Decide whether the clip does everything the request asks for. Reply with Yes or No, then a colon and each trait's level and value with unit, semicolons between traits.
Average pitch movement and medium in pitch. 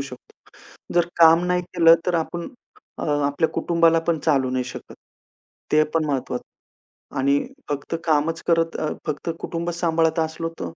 No: narrow, 2.3 semitones; medium, 165 Hz